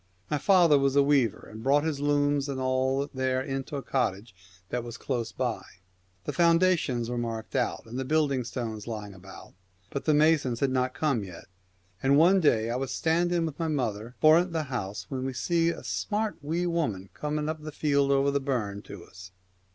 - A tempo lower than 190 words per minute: No, fast, 205 wpm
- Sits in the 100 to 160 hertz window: Yes, low, 135 Hz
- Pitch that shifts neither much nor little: Yes, average, 4.3 semitones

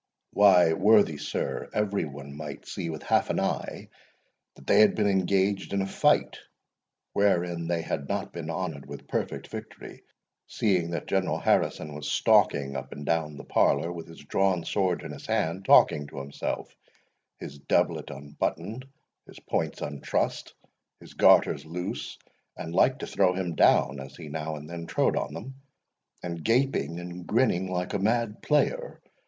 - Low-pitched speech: Yes, very low, 85 Hz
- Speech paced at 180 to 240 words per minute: No, average, 165 wpm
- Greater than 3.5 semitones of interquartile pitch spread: Yes, average, 4.6 semitones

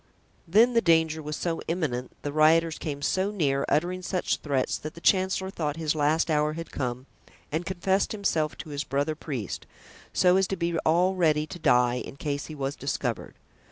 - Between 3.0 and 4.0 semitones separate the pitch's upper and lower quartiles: Yes, average, 3.6 semitones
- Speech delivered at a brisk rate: No, average, 190 wpm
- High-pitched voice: No, medium, 155 Hz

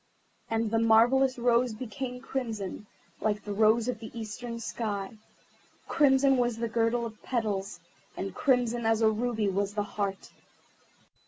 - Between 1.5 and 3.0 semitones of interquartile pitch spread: Yes, narrow, 2.4 semitones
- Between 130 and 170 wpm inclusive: Yes, average, 145 wpm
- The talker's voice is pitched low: No, high, 225 Hz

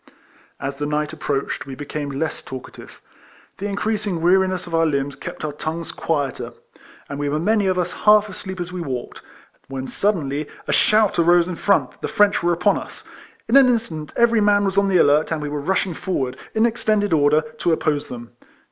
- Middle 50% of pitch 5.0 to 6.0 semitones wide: Yes, wide, 5.4 semitones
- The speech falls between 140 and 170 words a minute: No, average, 200 wpm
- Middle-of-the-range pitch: Yes, medium, 170 Hz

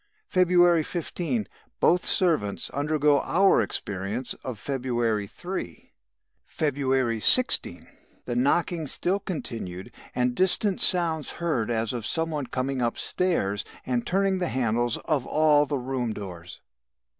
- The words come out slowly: Yes, slow, 120 wpm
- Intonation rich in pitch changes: Yes, wide, 6.4 semitones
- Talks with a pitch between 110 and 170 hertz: Yes, low, 135 Hz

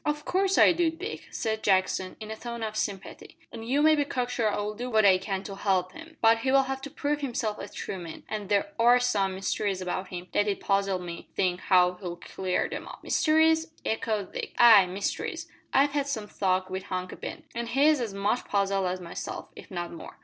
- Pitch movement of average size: No, wide, 5.7 semitones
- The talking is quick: Yes, fast, 220 wpm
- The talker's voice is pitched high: Yes, high, 210 Hz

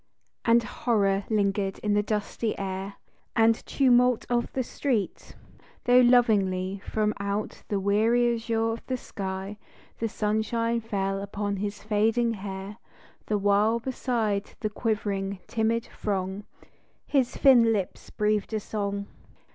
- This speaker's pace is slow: Yes, slow, 130 wpm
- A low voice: No, high, 210 Hz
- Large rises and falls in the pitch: No, narrow, 2.5 semitones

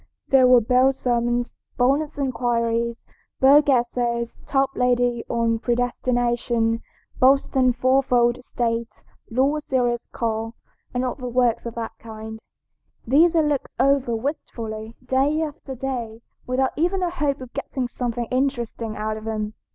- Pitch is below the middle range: No, high, 245 Hz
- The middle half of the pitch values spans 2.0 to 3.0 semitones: Yes, narrow, 2.4 semitones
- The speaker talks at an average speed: No, slow, 130 wpm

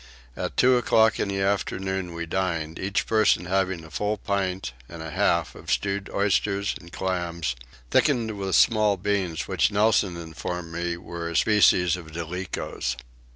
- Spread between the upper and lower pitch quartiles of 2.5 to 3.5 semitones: Yes, average, 3.0 semitones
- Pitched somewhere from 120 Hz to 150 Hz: No, very low, 95 Hz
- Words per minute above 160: No, average, 155 wpm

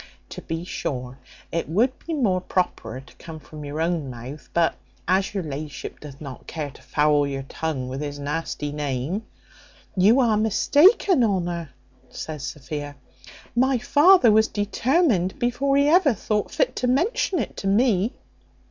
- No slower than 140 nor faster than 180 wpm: Yes, average, 160 wpm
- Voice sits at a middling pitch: Yes, medium, 175 Hz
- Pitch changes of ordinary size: No, wide, 8.6 semitones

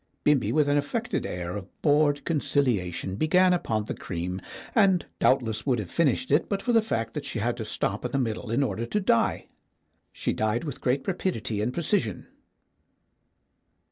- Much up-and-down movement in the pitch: Yes, wide, 7.6 semitones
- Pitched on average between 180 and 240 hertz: No, low, 135 Hz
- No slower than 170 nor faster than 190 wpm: Yes, average, 175 wpm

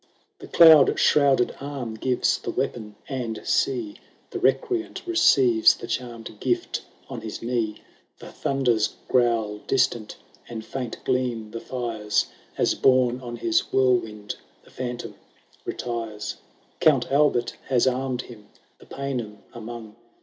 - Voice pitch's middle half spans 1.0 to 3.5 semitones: Yes, average, 2.9 semitones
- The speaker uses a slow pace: Yes, slow, 130 wpm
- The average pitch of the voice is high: No, low, 120 Hz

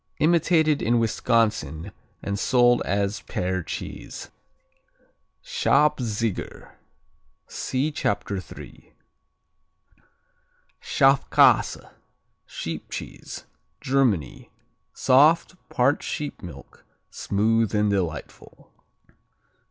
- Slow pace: Yes, slow, 70 wpm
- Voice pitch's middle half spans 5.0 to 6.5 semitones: Yes, wide, 5.4 semitones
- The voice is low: Yes, low, 115 Hz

